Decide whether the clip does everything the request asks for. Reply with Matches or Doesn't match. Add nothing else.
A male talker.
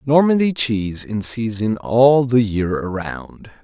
Matches